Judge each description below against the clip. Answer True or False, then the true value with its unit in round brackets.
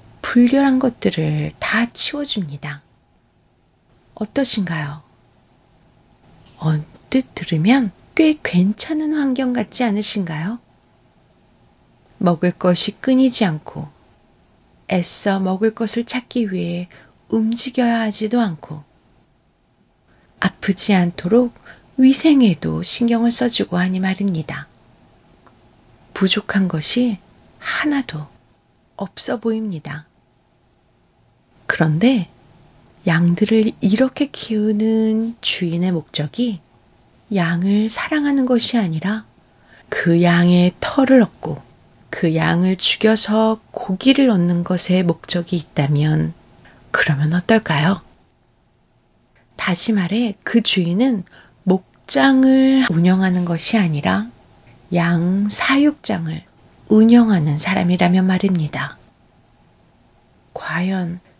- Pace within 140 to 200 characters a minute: True (195 characters per minute)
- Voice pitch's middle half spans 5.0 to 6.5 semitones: True (5.5 semitones)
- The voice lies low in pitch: False (190 Hz)